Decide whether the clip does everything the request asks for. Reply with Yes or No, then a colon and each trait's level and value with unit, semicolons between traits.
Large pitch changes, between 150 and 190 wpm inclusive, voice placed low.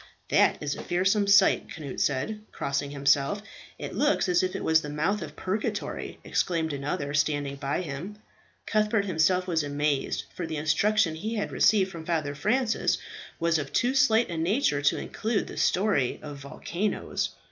No: wide, 6.0 semitones; average, 165 wpm; medium, 165 Hz